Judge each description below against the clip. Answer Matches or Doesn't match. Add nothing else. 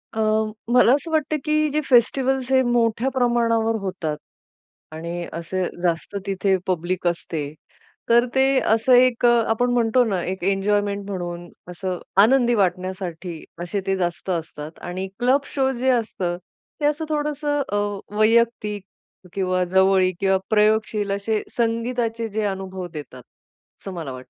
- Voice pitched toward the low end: Doesn't match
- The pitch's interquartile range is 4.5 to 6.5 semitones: Matches